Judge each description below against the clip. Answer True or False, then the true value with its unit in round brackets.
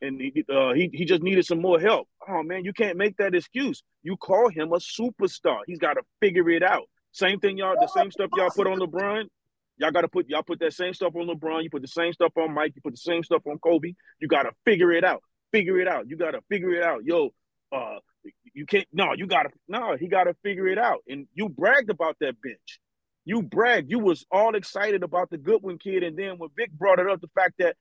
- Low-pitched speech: False (185 Hz)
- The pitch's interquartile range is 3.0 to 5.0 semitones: True (3.4 semitones)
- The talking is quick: True (255 wpm)